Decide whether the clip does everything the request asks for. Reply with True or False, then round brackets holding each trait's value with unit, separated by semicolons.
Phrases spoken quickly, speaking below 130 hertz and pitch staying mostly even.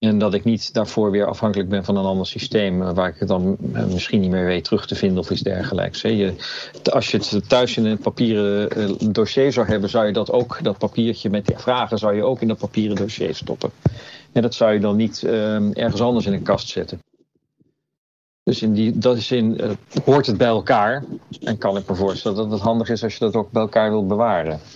True (230 wpm; 110 Hz; 2.2 semitones)